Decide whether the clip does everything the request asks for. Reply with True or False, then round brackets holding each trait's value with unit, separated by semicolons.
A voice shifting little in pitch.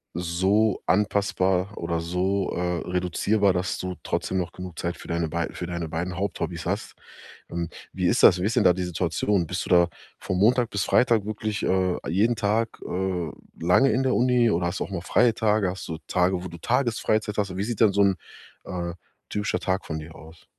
False (3.0 semitones)